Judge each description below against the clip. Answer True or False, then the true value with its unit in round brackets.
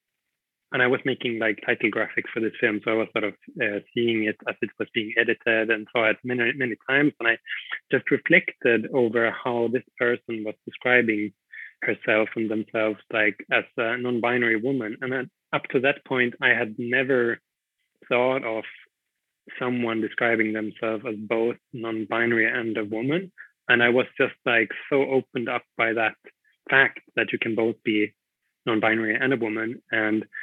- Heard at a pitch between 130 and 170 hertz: False (115 Hz)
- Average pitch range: False (2.0 semitones)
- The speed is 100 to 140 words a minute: False (175 wpm)